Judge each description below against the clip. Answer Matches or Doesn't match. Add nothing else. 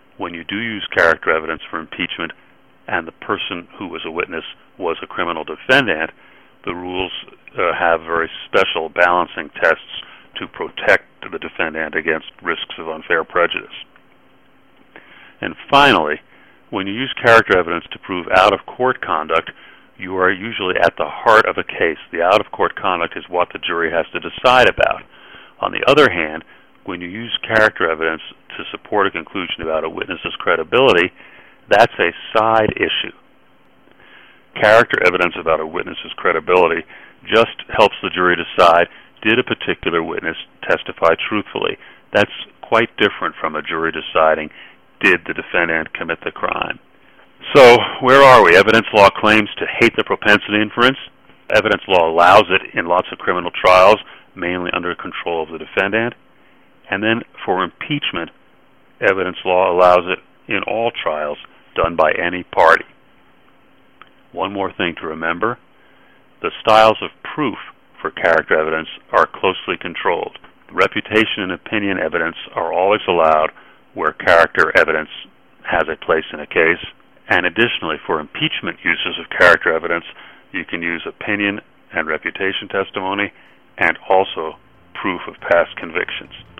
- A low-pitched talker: Matches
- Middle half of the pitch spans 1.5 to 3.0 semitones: Doesn't match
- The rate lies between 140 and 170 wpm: Matches